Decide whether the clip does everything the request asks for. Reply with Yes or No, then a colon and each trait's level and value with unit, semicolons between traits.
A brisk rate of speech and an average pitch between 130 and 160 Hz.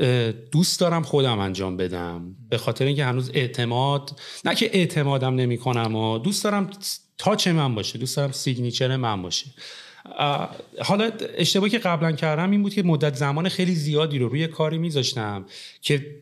No: average, 160 wpm; medium, 140 Hz